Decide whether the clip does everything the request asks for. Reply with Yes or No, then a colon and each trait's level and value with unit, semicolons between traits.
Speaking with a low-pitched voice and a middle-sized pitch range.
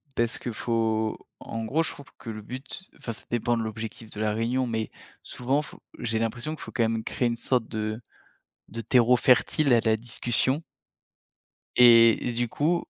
No: low, 115 Hz; narrow, 2.0 semitones